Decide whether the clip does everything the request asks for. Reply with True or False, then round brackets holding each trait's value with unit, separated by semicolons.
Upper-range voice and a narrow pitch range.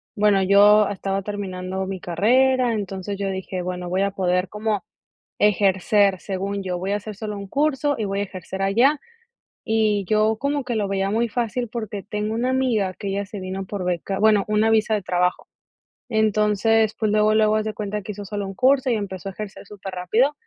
True (205 Hz; 2.1 semitones)